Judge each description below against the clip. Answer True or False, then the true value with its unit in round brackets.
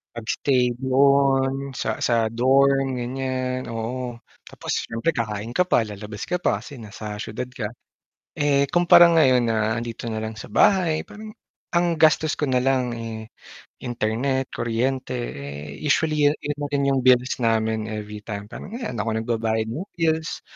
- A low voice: True (125 Hz)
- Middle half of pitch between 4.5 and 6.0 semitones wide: False (3.9 semitones)